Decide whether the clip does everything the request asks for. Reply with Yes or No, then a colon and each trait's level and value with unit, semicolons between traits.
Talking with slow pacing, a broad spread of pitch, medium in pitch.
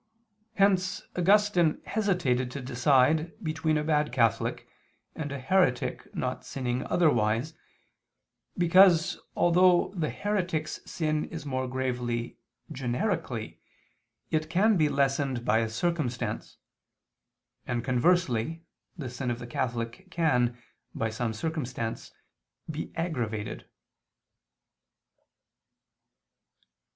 Yes: slow, 100 wpm; wide, 5.7 semitones; medium, 145 Hz